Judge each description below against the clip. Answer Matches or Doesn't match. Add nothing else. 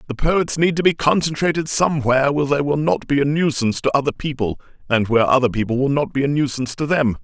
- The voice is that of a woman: Doesn't match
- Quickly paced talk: Matches